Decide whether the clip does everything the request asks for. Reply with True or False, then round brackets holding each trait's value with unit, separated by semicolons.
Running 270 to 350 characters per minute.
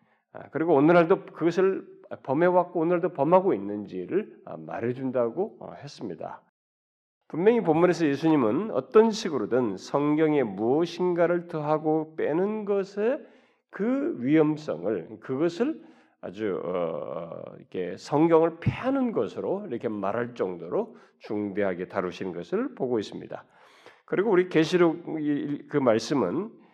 True (275 characters per minute)